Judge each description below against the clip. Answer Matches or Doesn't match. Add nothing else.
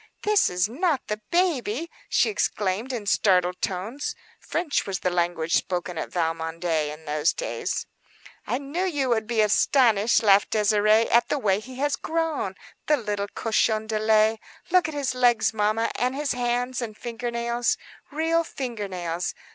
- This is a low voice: Doesn't match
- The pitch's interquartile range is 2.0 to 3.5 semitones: Doesn't match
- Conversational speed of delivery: Matches